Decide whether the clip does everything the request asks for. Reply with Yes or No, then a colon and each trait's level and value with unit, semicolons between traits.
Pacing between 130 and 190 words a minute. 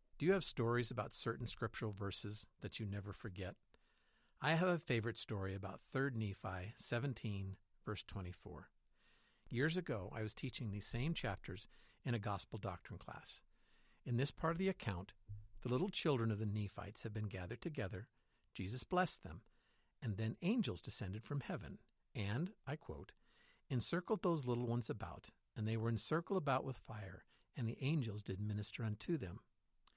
Yes: average, 165 wpm